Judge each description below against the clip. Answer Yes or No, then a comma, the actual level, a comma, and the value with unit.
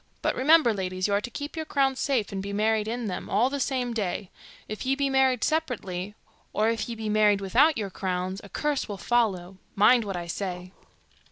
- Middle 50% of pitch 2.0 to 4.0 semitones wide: No, average, 4.9 semitones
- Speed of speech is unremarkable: No, fast, 210 wpm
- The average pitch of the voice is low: No, high, 215 Hz